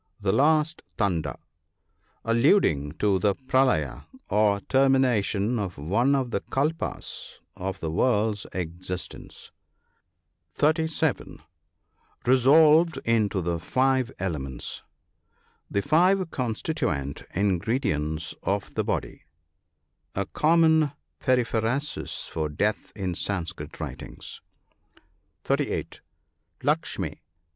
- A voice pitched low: Yes, low, 110 Hz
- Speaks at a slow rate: Yes, slow, 95 wpm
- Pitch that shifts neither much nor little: No, wide, 6.8 semitones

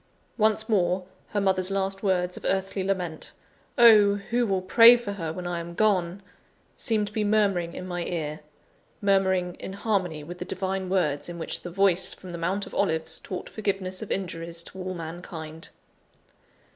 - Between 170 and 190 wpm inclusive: Yes, average, 175 wpm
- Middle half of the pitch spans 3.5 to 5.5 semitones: No, narrow, 2.5 semitones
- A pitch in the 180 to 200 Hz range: Yes, medium, 185 Hz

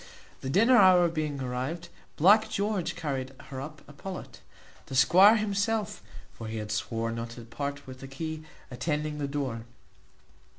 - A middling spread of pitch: No, wide, 6.0 semitones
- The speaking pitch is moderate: Yes, medium, 150 Hz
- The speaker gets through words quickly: No, average, 160 wpm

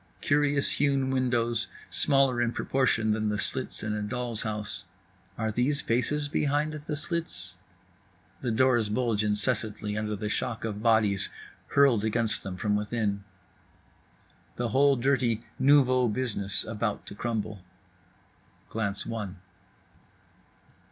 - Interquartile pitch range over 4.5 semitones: No, average, 3.8 semitones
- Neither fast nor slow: No, slow, 125 wpm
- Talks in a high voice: No, low, 115 Hz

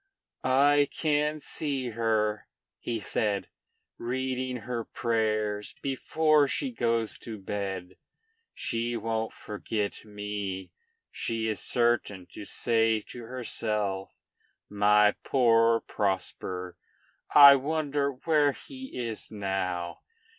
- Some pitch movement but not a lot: Yes, average, 4.0 semitones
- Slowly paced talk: Yes, slow, 100 wpm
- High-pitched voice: No, low, 115 Hz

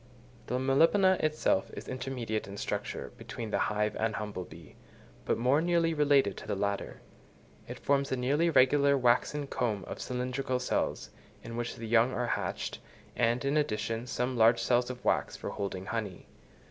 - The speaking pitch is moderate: No, low, 125 Hz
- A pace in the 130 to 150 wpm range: No, average, 170 wpm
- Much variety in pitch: No, average, 4.0 semitones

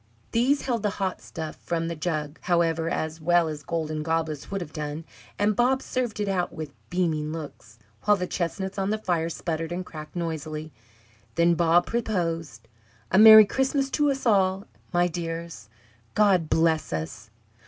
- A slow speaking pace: No, average, 165 wpm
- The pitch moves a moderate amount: Yes, average, 3.9 semitones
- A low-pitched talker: No, medium, 170 Hz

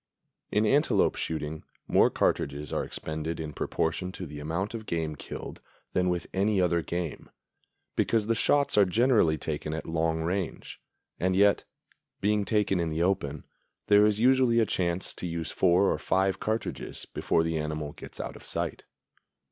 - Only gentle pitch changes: No, average, 4.4 semitones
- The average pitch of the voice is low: Yes, very low, 90 Hz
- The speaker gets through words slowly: No, average, 165 wpm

